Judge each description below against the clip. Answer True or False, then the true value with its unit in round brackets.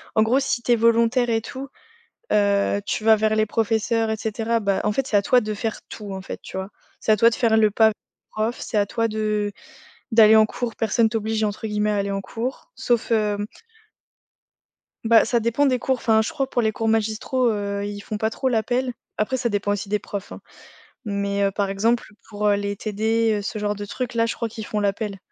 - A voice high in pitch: True (220 Hz)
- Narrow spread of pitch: True (2.0 semitones)